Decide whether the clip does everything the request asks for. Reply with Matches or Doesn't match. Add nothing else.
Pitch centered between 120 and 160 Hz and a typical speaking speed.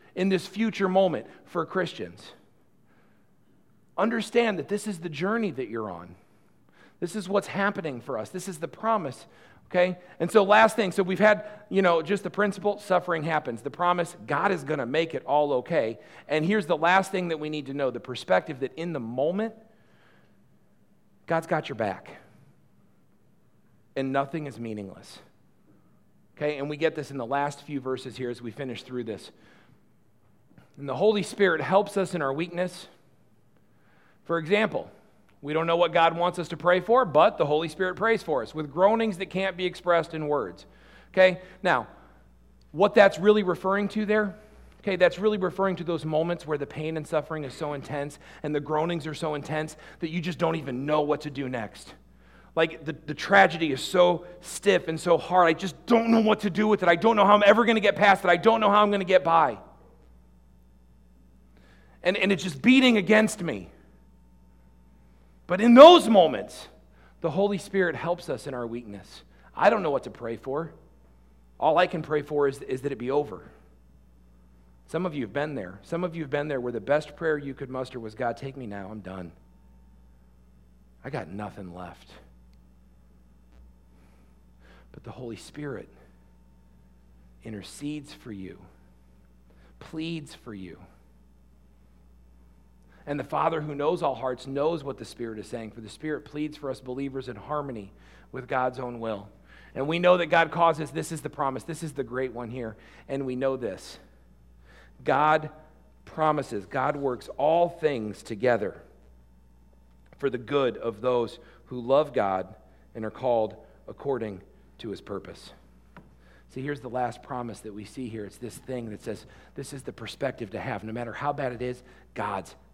Matches